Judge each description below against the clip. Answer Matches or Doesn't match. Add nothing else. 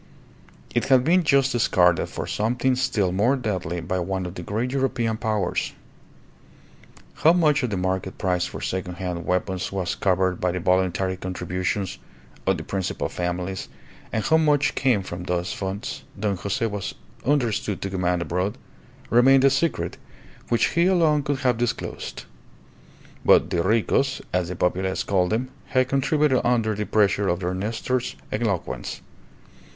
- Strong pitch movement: Matches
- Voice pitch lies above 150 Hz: Doesn't match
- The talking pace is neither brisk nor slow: Matches